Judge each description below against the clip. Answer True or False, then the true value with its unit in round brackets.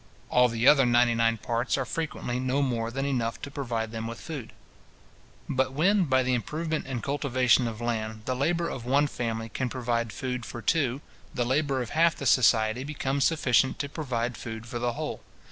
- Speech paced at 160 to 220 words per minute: True (195 wpm)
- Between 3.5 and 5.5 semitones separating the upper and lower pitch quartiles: False (3.1 semitones)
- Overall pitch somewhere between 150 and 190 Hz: False (125 Hz)